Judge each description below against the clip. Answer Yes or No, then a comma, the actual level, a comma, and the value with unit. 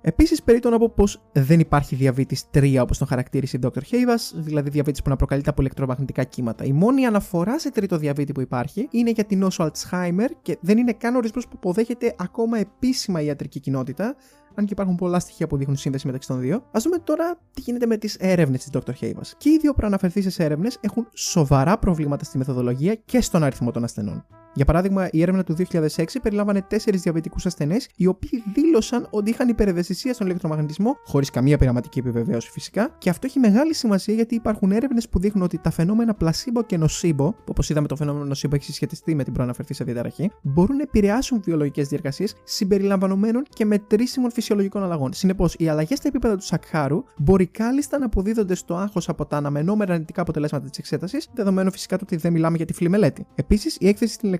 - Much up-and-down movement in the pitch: Yes, wide, 7.0 semitones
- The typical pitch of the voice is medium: Yes, medium, 180 Hz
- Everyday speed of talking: No, fast, 200 wpm